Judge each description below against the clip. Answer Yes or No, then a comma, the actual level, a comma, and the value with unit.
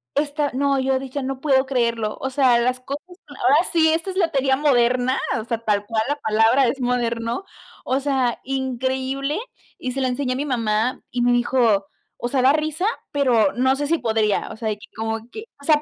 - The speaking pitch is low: No, very high, 260 Hz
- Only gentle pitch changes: No, average, 3.0 semitones